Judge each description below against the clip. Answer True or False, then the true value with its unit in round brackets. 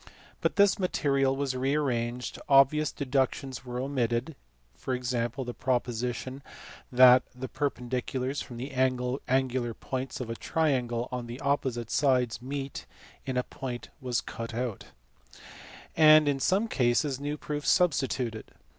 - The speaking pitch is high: False (130 Hz)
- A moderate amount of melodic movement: False (2.2 semitones)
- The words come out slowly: True (130 wpm)